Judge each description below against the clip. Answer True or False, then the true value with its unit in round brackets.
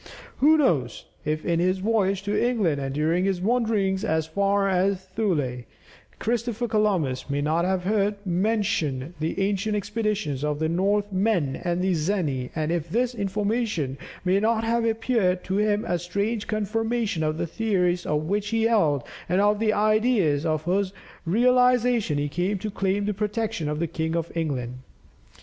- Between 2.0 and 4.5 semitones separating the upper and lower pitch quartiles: False (5.0 semitones)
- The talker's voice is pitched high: True (195 Hz)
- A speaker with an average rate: True (165 wpm)